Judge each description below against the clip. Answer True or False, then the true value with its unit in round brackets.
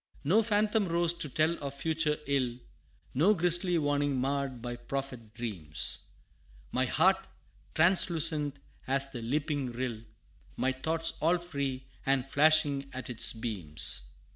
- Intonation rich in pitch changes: False (4.4 semitones)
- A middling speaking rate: False (130 wpm)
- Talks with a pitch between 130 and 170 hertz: True (140 Hz)